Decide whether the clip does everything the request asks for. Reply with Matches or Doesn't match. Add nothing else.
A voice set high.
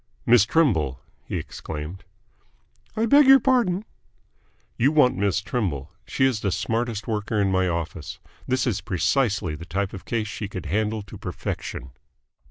Doesn't match